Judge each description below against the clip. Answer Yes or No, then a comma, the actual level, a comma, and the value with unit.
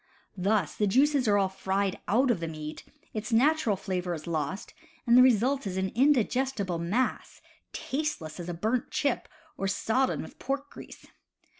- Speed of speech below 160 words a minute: No, average, 165 wpm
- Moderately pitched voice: No, high, 210 Hz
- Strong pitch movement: Yes, wide, 5.8 semitones